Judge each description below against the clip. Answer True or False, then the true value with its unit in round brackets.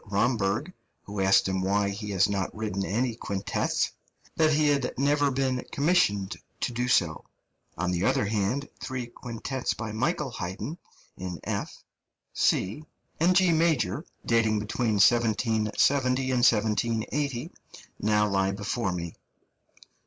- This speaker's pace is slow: True (130 wpm)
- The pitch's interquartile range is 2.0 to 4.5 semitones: False (5.0 semitones)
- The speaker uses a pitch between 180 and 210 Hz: False (110 Hz)